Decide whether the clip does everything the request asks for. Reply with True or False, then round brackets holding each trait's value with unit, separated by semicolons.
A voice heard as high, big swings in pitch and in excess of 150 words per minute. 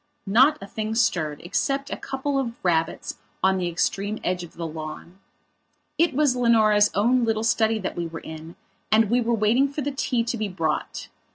True (215 Hz; 5.8 semitones; 190 wpm)